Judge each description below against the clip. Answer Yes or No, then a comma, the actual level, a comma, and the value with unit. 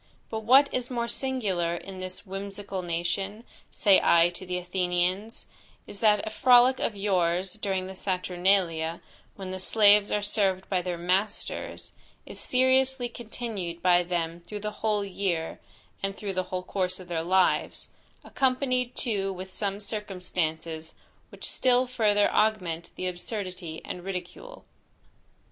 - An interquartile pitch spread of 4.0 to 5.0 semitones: No, average, 3.2 semitones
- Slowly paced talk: No, average, 145 wpm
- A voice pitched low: No, high, 195 Hz